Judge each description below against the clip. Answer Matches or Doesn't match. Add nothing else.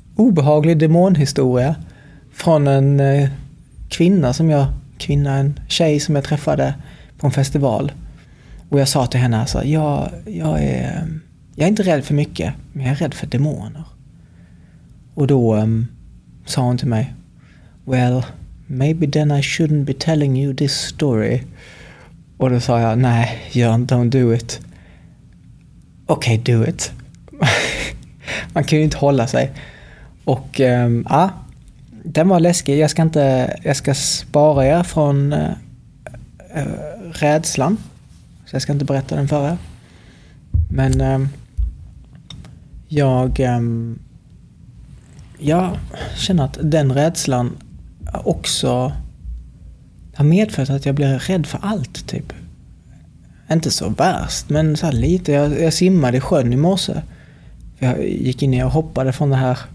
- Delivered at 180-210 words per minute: Doesn't match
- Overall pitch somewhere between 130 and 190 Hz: Matches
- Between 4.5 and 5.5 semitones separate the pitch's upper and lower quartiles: Doesn't match